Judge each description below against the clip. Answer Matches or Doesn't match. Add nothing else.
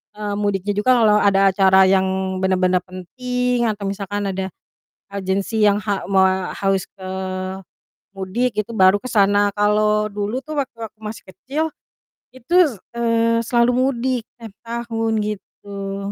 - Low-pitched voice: Doesn't match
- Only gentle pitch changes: Doesn't match